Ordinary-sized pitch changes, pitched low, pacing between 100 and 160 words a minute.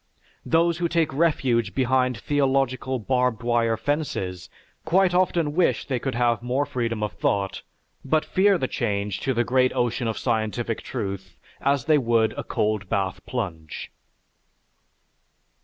Yes: average, 4.5 semitones; low, 125 Hz; average, 140 wpm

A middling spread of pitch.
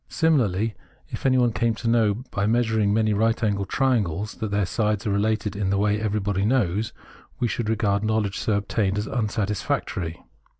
No: narrow, 2.1 semitones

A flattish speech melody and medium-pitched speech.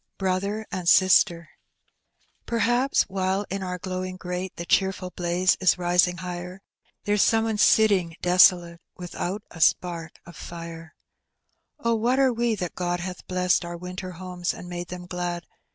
Yes: narrow, 1.7 semitones; medium, 180 Hz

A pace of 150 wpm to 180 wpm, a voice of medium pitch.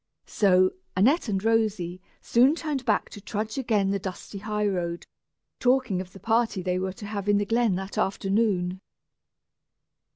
No: average, 160 wpm; high, 205 Hz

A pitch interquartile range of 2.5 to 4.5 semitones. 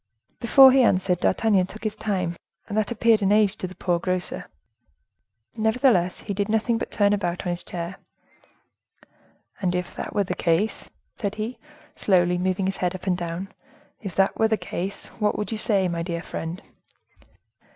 Yes: average, 3.2 semitones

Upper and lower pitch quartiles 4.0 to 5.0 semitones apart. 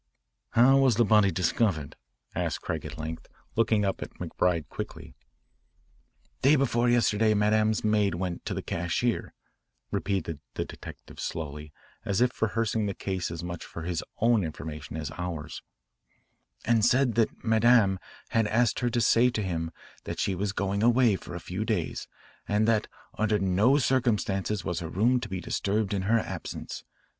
Yes: average, 4.3 semitones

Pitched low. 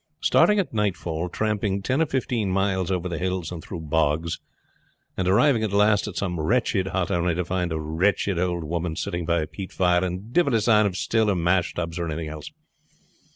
Yes: very low, 90 Hz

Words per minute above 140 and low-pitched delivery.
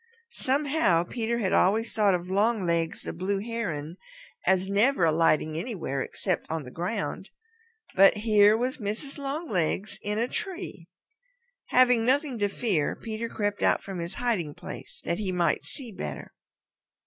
No: average, 150 wpm; high, 205 Hz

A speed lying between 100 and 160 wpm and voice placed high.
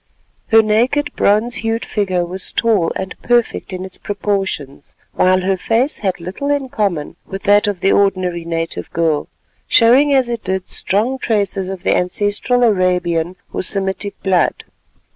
Yes: average, 155 wpm; high, 195 Hz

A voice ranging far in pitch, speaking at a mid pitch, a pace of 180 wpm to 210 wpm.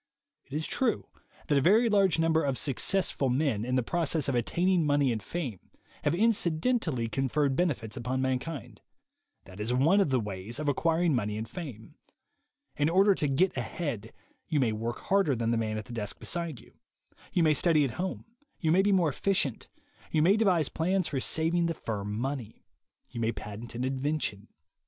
Yes: wide, 6.4 semitones; medium, 145 Hz; average, 190 wpm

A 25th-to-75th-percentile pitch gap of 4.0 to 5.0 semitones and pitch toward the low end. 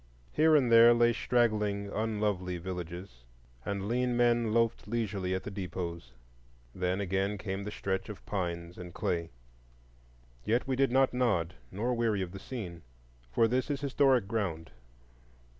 Yes: average, 4.4 semitones; low, 105 Hz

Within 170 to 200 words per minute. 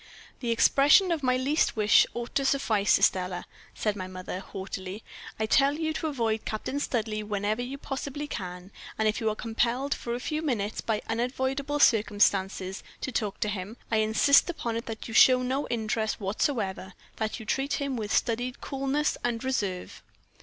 Yes: average, 175 wpm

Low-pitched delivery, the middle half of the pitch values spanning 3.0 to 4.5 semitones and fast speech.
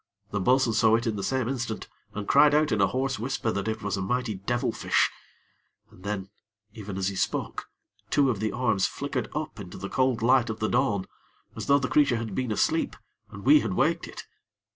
Yes: low, 115 Hz; average, 4.1 semitones; fast, 210 wpm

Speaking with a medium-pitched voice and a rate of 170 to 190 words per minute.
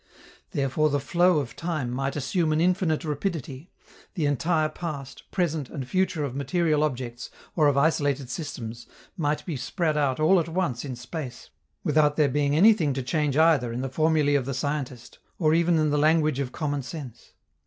Yes: medium, 150 Hz; average, 180 wpm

